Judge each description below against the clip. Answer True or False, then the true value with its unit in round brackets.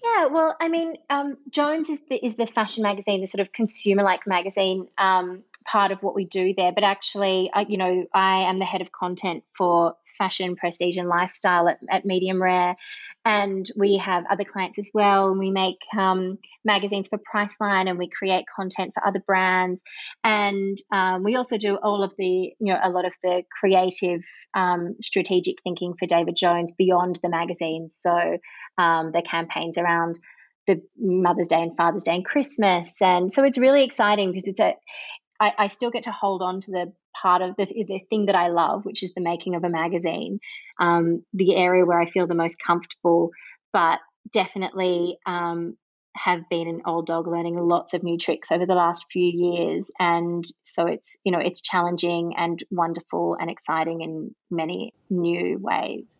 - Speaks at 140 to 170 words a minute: False (185 wpm)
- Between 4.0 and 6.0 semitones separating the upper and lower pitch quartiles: False (2.5 semitones)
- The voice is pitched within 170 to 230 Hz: True (185 Hz)